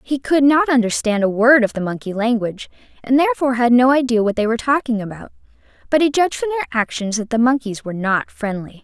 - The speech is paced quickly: Yes, fast, 215 wpm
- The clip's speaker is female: Yes, female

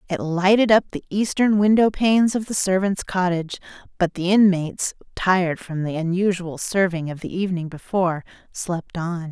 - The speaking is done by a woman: Yes, female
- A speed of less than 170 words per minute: Yes, average, 160 wpm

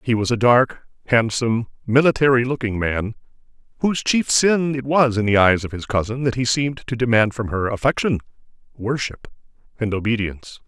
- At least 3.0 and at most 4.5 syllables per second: No, 5.5 syllables/s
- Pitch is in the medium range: No, low, 120 Hz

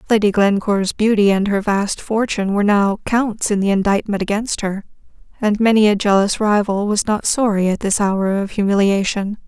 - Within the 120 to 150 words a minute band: No, average, 175 wpm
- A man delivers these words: No, female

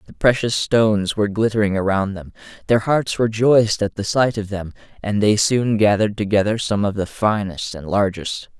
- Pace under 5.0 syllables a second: No, 5.2 syllables/s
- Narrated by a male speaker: Yes, male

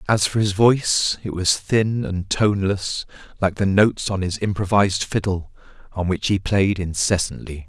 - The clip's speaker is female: No, male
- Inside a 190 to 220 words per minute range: No, average, 165 wpm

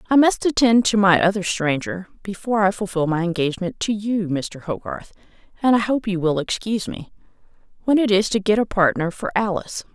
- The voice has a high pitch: Yes, high, 195 Hz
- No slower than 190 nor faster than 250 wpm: Yes, average, 195 wpm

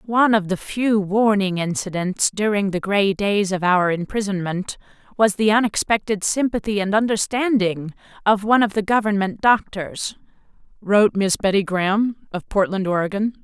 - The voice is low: No, high, 200 Hz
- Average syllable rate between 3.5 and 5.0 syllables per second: Yes, 4.8 syllables/s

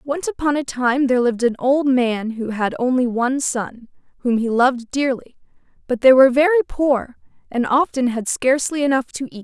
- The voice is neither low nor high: No, very high, 255 Hz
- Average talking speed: Yes, average, 190 wpm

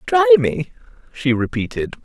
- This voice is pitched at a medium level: Yes, medium, 165 Hz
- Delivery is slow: Yes, slow, 120 wpm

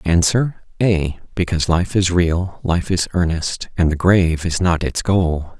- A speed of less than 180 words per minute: Yes, average, 170 wpm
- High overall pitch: No, very low, 90 Hz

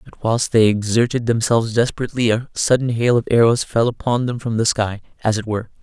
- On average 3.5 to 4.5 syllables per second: No, 6.0 syllables/s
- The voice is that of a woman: No, male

